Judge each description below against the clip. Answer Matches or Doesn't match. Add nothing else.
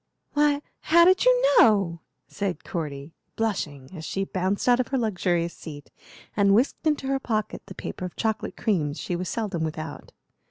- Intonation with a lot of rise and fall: Matches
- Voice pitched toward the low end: Doesn't match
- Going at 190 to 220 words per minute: Doesn't match